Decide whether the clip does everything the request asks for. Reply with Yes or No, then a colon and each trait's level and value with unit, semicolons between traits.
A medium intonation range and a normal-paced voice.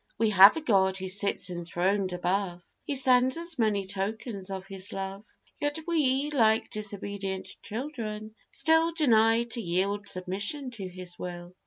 Yes: average, 4.6 semitones; average, 150 wpm